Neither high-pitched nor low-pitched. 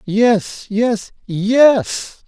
No: high, 220 Hz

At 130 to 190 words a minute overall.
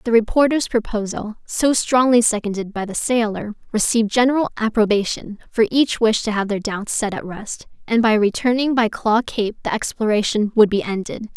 Yes: average, 175 wpm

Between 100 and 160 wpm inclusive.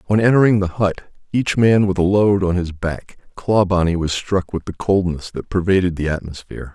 No: average, 195 wpm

